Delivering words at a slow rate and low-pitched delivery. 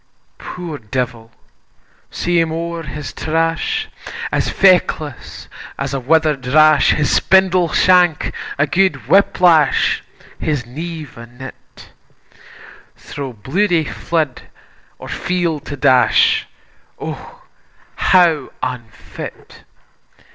No: slow, 100 wpm; medium, 155 Hz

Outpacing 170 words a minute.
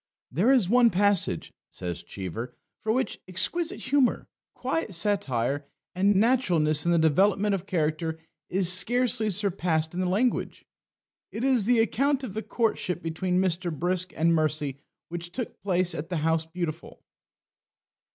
No: average, 145 wpm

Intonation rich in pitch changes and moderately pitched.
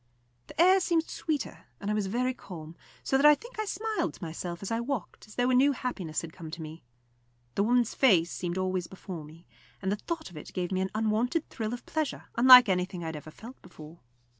No: wide, 6.8 semitones; high, 210 Hz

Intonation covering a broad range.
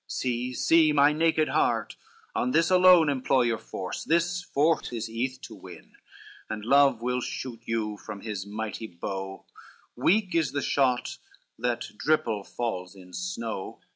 Yes: wide, 5.9 semitones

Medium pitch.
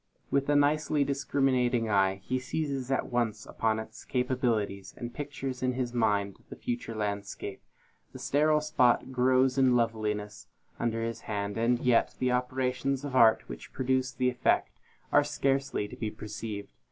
No: low, 125 Hz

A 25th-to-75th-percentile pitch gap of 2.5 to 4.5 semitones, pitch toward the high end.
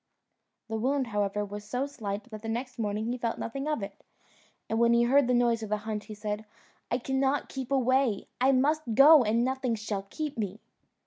Yes: average, 3.8 semitones; high, 235 Hz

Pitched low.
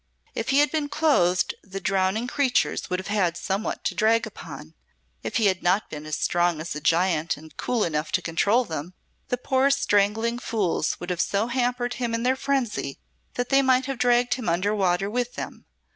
No: high, 210 Hz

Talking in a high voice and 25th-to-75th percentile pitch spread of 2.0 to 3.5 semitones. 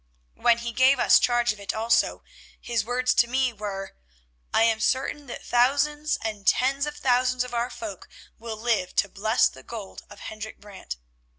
Yes: high, 235 Hz; average, 2.8 semitones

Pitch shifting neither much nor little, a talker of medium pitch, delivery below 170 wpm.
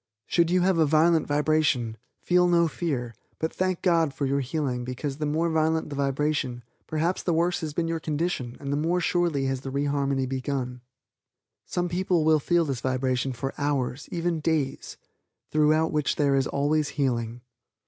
No: average, 3.5 semitones; medium, 150 Hz; average, 180 wpm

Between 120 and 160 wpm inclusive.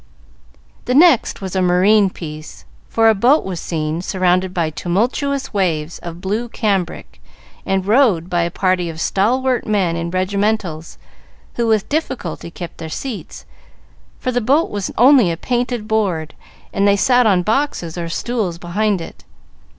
Yes: average, 155 wpm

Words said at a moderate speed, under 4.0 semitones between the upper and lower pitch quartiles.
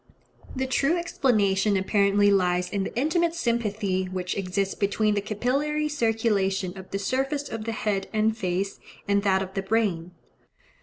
Yes: average, 155 wpm; average, 3.6 semitones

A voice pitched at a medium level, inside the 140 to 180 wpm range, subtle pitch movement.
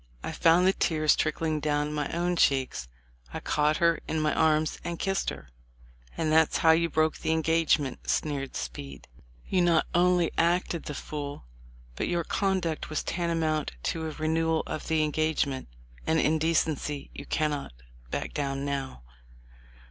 Yes: medium, 155 Hz; average, 155 wpm; narrow, 2.0 semitones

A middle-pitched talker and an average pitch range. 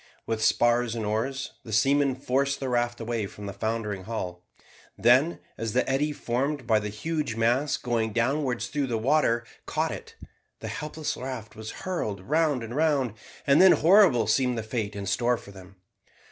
No: low, 120 Hz; average, 3.9 semitones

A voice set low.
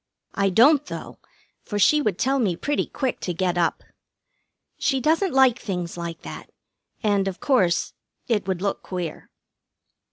No: high, 200 Hz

